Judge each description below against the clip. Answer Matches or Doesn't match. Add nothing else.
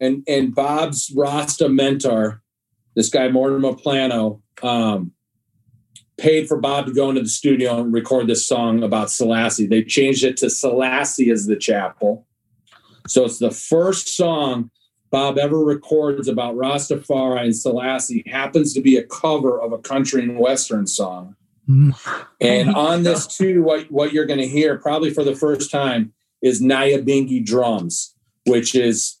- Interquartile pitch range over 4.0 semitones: Doesn't match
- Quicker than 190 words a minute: Doesn't match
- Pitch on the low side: Matches